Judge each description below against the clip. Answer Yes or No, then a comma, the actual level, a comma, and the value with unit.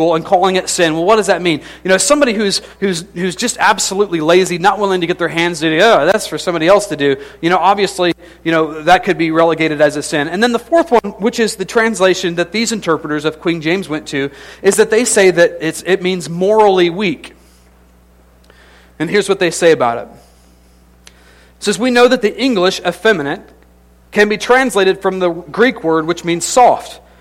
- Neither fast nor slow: No, fast, 210 wpm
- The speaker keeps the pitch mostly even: No, average, 4.4 semitones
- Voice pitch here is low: No, medium, 175 Hz